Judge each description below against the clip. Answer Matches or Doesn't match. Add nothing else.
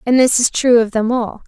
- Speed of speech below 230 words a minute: Doesn't match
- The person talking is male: Doesn't match